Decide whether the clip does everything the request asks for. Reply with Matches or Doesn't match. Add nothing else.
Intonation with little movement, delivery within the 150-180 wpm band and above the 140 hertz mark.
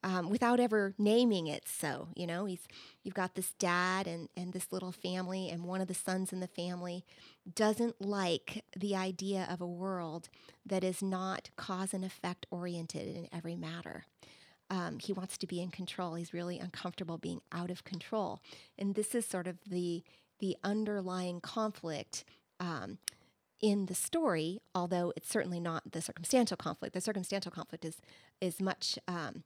Matches